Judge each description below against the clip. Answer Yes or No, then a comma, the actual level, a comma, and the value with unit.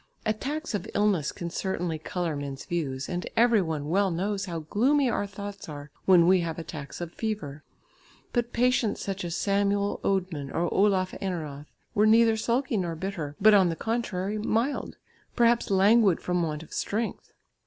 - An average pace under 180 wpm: Yes, average, 165 wpm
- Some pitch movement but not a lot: Yes, average, 4.5 semitones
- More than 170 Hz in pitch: Yes, high, 190 Hz